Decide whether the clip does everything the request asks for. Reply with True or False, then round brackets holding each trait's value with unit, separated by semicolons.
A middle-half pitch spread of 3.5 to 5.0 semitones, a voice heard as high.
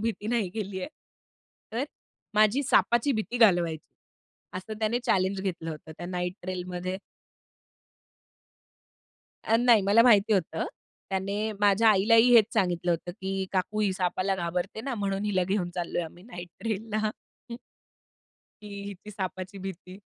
False (3.0 semitones; 195 Hz)